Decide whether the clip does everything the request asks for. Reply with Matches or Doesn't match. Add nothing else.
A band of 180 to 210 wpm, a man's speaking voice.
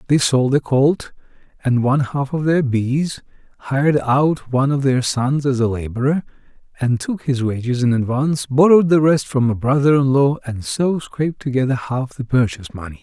Matches